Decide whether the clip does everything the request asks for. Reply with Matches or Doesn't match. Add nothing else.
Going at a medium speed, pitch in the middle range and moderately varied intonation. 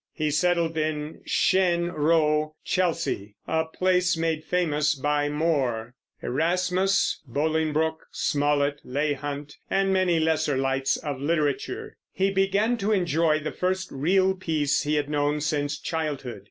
Doesn't match